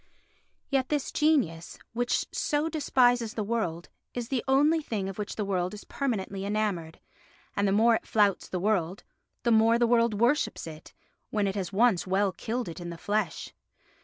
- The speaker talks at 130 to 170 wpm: No, average, 180 wpm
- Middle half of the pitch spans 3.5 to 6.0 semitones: Yes, average, 4.1 semitones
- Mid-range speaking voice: No, high, 215 Hz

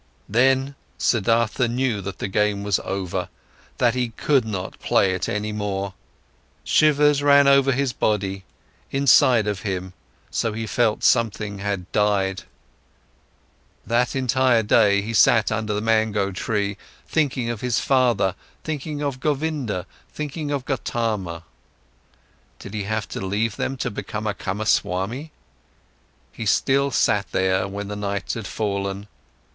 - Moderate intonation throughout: Yes, average, 4.4 semitones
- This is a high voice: No, low, 110 Hz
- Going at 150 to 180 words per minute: No, average, 140 wpm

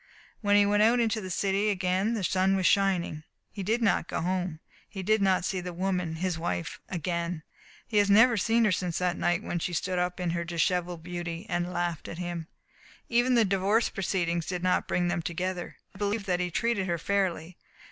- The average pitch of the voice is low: No, medium, 185 Hz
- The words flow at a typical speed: No, fast, 210 wpm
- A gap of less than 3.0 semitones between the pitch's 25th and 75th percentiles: Yes, narrow, 2.5 semitones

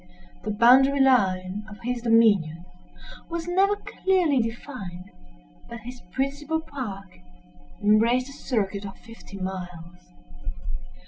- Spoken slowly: Yes, slow, 110 wpm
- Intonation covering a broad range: Yes, wide, 5.7 semitones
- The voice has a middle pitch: No, high, 230 Hz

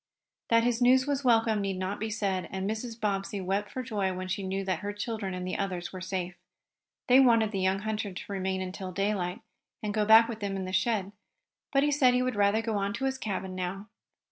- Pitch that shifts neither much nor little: Yes, average, 3.1 semitones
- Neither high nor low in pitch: No, high, 205 Hz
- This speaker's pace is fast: Yes, fast, 230 wpm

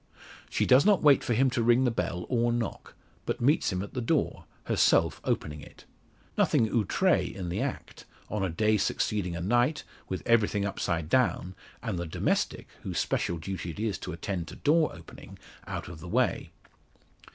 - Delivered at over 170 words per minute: Yes, average, 185 wpm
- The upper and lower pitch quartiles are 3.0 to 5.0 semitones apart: No, wide, 5.5 semitones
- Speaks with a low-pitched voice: Yes, low, 105 Hz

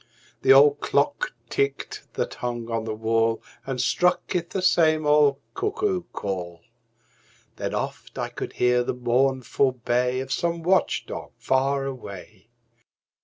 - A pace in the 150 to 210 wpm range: No, average, 140 wpm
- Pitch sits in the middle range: No, low, 130 Hz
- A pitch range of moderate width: Yes, average, 4.0 semitones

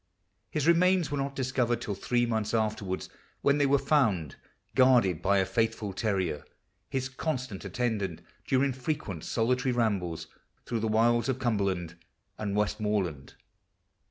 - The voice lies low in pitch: Yes, low, 115 Hz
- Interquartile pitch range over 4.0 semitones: Yes, average, 5.0 semitones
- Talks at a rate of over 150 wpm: No, average, 145 wpm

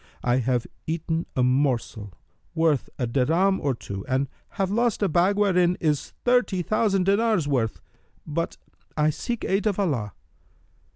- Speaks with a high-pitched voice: No, medium, 165 Hz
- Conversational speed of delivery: Yes, average, 150 wpm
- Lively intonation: Yes, wide, 7.1 semitones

